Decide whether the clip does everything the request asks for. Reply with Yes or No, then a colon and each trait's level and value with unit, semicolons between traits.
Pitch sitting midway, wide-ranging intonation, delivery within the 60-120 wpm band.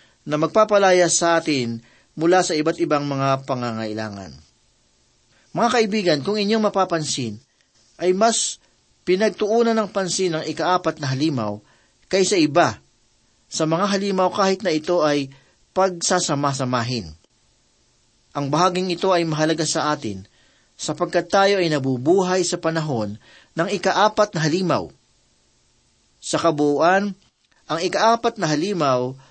Yes: medium, 165 Hz; wide, 5.7 semitones; average, 115 wpm